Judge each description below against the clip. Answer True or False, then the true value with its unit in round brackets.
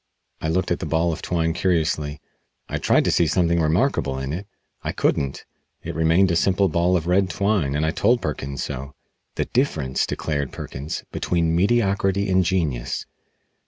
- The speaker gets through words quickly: False (170 wpm)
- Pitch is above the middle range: False (85 Hz)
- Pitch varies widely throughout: False (3.8 semitones)